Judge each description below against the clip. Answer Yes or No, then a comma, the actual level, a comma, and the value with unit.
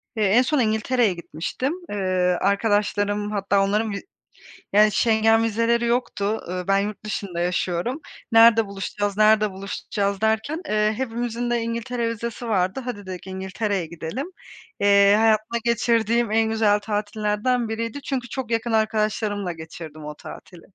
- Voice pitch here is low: No, high, 215 Hz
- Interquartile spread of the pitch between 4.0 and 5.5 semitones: No, narrow, 2.5 semitones